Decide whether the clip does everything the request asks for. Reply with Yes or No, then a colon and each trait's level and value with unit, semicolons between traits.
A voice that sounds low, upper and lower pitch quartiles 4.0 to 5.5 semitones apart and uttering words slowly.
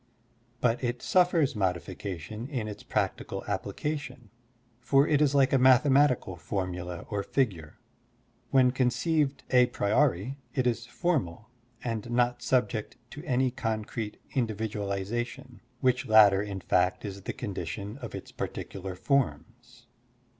Yes: low, 120 Hz; average, 4.6 semitones; slow, 125 wpm